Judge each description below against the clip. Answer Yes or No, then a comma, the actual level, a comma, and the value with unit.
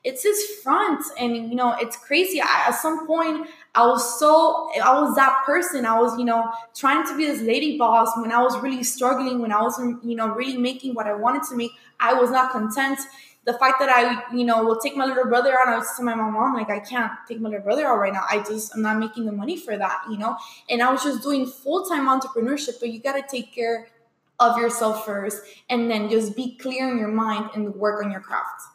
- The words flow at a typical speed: No, fast, 245 wpm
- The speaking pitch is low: No, high, 245 Hz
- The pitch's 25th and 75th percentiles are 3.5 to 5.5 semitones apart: No, average, 3.0 semitones